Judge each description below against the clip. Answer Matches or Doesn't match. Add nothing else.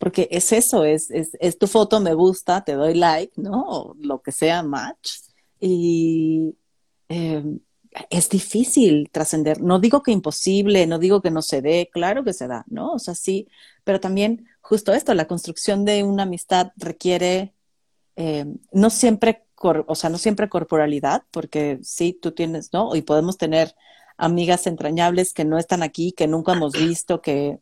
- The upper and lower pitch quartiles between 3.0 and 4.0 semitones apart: Matches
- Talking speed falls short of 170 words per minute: Doesn't match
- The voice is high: Doesn't match